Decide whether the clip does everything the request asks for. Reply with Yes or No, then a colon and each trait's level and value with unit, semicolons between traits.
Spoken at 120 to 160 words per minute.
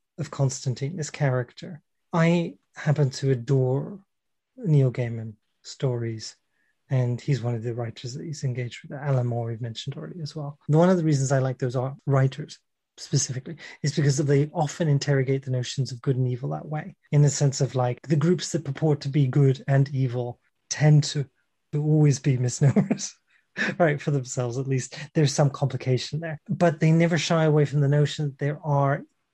No: average, 185 wpm